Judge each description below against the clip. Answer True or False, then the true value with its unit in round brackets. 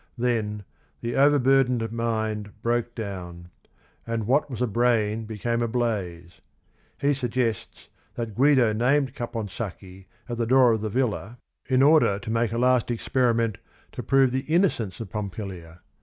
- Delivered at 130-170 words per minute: True (145 wpm)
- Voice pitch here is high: False (115 Hz)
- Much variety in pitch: False (3.1 semitones)